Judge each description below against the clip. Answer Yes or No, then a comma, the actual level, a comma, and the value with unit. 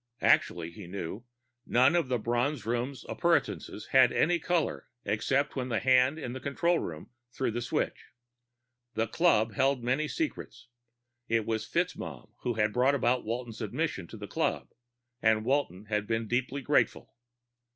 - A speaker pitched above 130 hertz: No, low, 120 Hz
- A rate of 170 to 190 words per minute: No, average, 155 wpm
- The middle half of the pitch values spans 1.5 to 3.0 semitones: No, average, 3.8 semitones